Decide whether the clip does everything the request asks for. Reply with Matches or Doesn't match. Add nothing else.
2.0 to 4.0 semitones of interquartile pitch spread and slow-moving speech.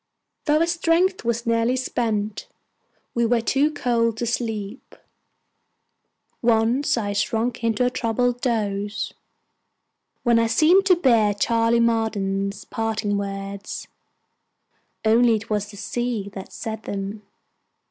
Matches